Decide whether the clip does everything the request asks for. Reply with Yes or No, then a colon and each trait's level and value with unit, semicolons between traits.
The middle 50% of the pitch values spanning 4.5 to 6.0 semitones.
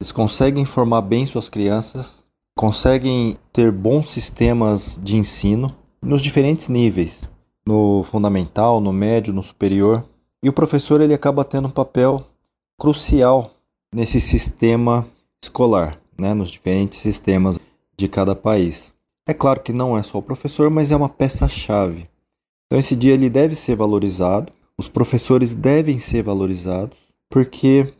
Yes: average, 4.8 semitones